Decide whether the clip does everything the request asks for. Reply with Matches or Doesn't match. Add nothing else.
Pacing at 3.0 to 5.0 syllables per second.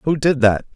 Matches